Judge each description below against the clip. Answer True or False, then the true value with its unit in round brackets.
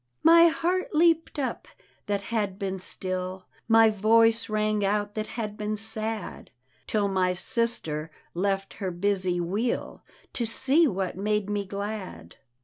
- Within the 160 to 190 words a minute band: False (140 wpm)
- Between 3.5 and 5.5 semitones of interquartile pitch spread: False (2.9 semitones)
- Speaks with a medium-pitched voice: False (210 Hz)